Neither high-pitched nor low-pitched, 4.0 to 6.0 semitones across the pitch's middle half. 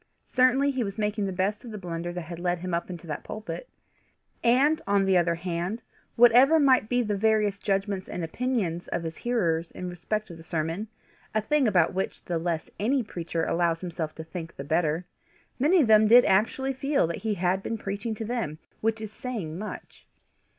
No: high, 195 Hz; average, 5.0 semitones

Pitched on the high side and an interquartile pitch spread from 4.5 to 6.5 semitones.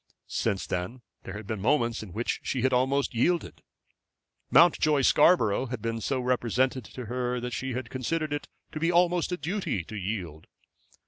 No: low, 125 Hz; average, 4.8 semitones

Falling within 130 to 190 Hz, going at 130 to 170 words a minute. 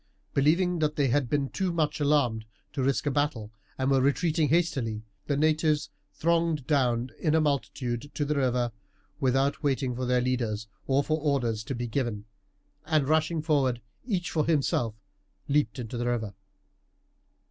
Yes: medium, 140 Hz; average, 160 wpm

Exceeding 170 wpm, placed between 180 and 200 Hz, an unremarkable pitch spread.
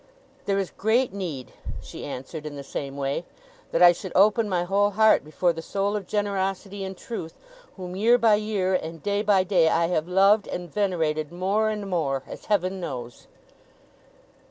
Yes: average, 180 wpm; high, 190 Hz; average, 3.7 semitones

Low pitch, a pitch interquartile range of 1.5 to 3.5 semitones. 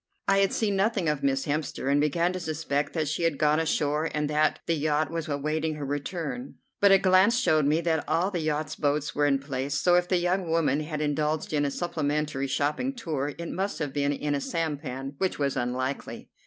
No: medium, 155 Hz; average, 2.9 semitones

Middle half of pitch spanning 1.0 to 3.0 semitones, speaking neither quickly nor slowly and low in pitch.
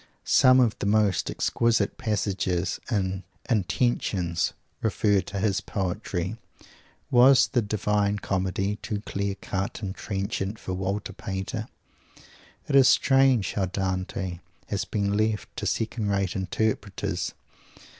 No: narrow, 2.5 semitones; slow, 120 wpm; low, 100 Hz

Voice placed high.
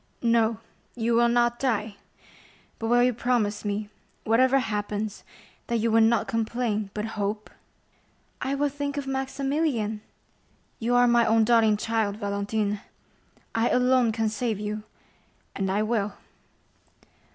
Yes: high, 225 Hz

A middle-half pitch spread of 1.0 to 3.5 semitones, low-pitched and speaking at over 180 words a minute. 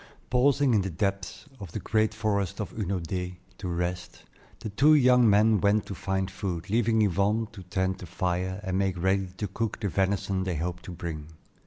Yes: average, 2.9 semitones; very low, 95 Hz; average, 190 wpm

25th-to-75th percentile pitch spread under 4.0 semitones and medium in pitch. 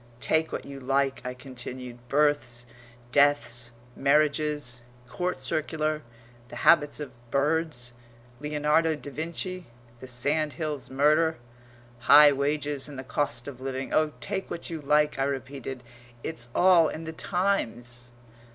Yes: average, 3.0 semitones; medium, 145 Hz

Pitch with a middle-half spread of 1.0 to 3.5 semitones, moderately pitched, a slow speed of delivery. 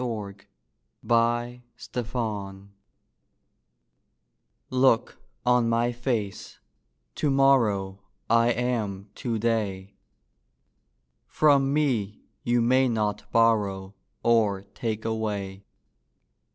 No: average, 3.2 semitones; low, 115 Hz; slow, 80 wpm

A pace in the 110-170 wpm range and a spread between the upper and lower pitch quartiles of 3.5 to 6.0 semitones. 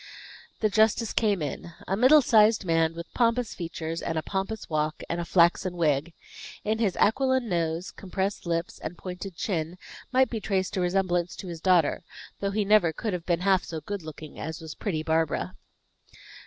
No: average, 180 wpm; average, 4.1 semitones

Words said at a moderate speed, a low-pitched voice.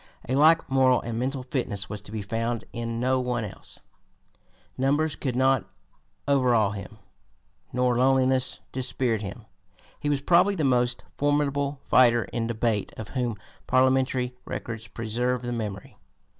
Yes: average, 145 wpm; low, 125 Hz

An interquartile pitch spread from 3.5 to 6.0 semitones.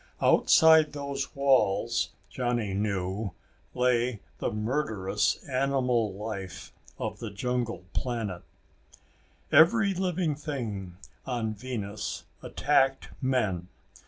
Yes: average, 5.0 semitones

